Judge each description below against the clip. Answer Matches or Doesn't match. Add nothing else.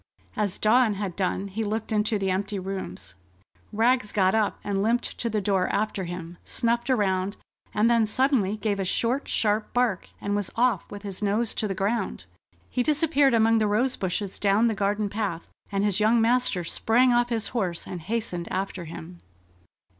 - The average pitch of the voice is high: Matches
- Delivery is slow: Doesn't match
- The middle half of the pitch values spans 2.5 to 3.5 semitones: Matches